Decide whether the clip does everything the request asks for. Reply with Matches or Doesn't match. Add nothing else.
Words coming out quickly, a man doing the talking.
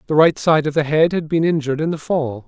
Matches